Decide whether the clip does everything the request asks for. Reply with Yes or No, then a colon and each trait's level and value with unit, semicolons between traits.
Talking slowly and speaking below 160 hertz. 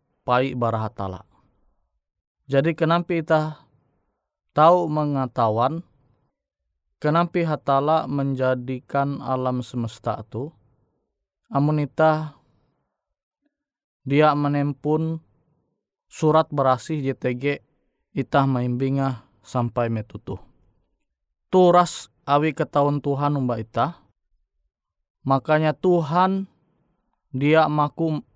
Yes: slow, 70 wpm; medium, 140 Hz